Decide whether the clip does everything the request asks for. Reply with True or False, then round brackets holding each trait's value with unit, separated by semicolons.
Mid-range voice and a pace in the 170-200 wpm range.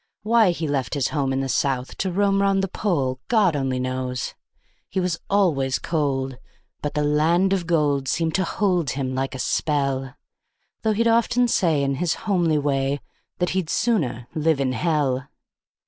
True (150 Hz; 175 wpm)